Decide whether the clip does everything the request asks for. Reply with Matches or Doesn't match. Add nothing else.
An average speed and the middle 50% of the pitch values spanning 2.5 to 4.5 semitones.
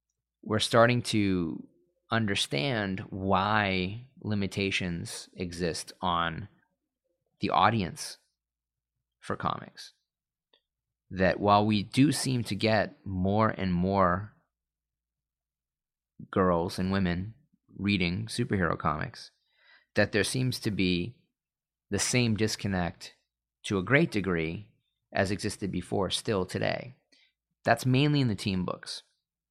Doesn't match